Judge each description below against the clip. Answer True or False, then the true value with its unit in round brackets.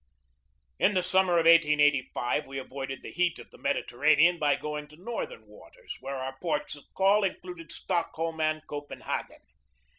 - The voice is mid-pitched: True (155 Hz)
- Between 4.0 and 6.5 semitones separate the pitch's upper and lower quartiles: False (3.6 semitones)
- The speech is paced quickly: False (155 wpm)